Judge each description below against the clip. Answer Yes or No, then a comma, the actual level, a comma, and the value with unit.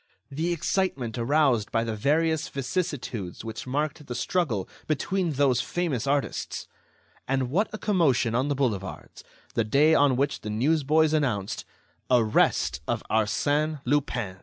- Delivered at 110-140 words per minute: Yes, slow, 135 wpm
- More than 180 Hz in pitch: No, low, 135 Hz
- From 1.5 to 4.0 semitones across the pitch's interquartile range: No, average, 5.1 semitones